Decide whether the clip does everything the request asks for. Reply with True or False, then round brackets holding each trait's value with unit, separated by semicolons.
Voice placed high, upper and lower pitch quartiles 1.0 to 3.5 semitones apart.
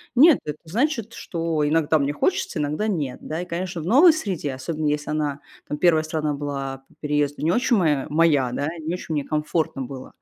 False (155 Hz; 3.2 semitones)